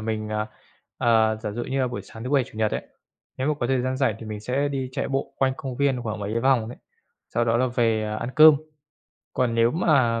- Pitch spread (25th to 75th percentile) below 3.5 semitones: Yes, average, 3.1 semitones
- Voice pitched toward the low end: Yes, low, 120 Hz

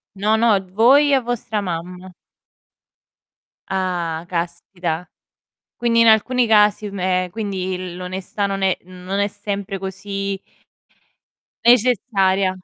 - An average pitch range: Yes, average, 3.0 semitones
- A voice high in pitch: Yes, high, 195 Hz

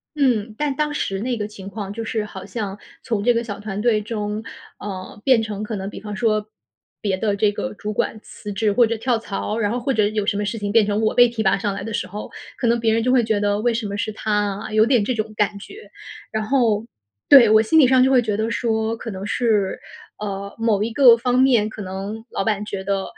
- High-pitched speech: Yes, high, 215 Hz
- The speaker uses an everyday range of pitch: No, narrow, 2.2 semitones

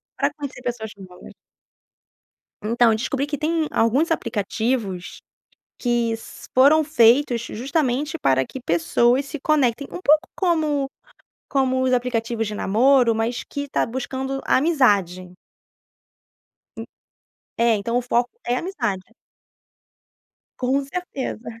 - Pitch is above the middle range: Yes, very high, 250 Hz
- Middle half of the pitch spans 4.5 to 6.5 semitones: No, average, 3.8 semitones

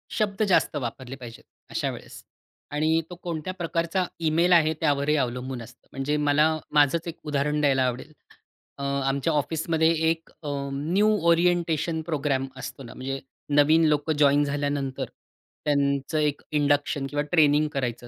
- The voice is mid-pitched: Yes, medium, 145 Hz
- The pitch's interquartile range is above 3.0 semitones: No, average, 2.7 semitones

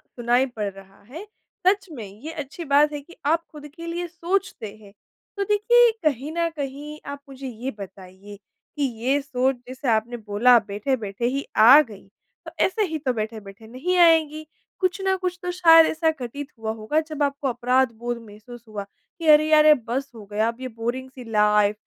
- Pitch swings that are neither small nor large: No, wide, 6.0 semitones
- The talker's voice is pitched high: Yes, very high, 270 Hz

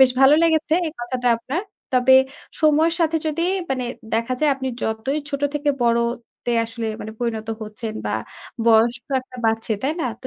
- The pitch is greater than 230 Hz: Yes, very high, 255 Hz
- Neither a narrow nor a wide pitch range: Yes, average, 4.2 semitones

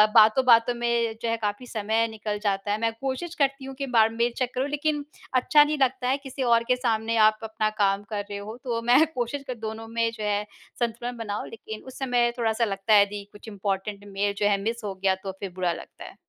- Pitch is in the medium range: No, high, 225 Hz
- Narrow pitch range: No, average, 3.2 semitones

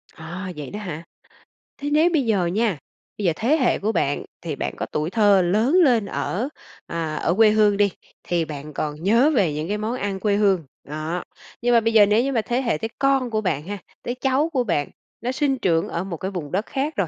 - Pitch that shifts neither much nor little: No, wide, 5.9 semitones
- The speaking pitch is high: Yes, high, 205 Hz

